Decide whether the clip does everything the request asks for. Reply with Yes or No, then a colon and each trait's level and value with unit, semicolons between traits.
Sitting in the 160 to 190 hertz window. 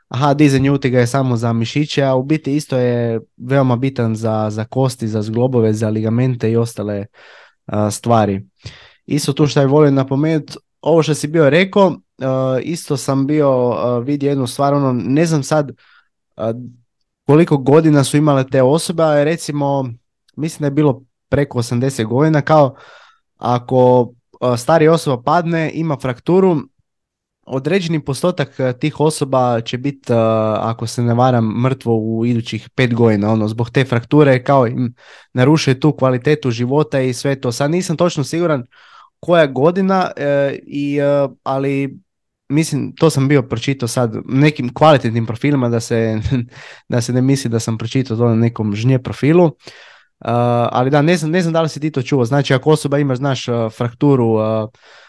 No: low, 130 Hz